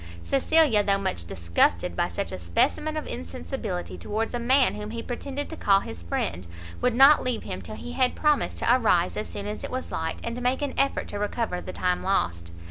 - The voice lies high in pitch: Yes, high, 215 Hz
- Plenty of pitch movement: Yes, wide, 7.9 semitones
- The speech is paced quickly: Yes, fast, 215 wpm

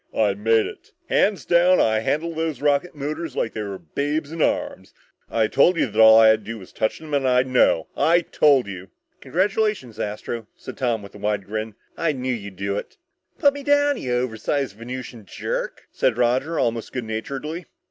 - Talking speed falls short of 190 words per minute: No, average, 200 wpm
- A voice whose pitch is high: No, low, 125 Hz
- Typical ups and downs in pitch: No, wide, 6.1 semitones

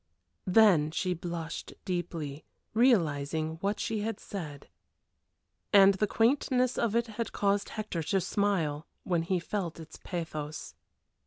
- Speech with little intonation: No, average, 4.7 semitones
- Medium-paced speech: No, slow, 125 wpm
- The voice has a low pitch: No, medium, 185 Hz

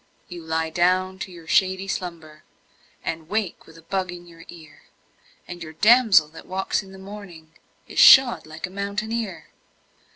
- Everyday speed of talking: Yes, average, 165 wpm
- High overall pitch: No, medium, 180 Hz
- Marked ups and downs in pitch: No, average, 3.2 semitones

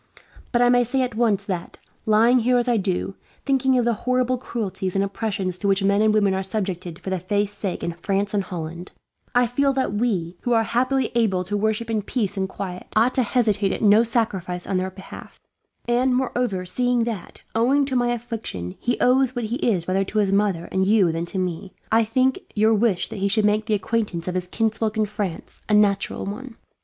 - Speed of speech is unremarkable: No, fast, 220 wpm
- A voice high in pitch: Yes, high, 210 Hz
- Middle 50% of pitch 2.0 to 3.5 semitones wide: No, average, 4.0 semitones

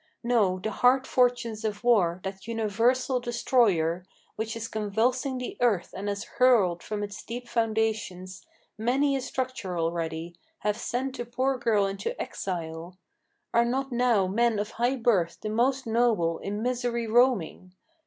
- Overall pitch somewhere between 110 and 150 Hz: No, high, 225 Hz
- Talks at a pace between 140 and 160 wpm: Yes, average, 150 wpm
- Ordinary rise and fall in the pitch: Yes, average, 4.0 semitones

